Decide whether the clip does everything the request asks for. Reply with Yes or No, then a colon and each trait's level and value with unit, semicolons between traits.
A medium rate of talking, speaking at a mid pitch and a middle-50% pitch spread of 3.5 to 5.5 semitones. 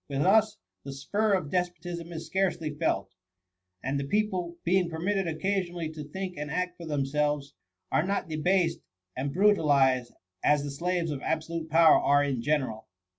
Yes: average, 170 wpm; medium, 160 Hz; average, 4.0 semitones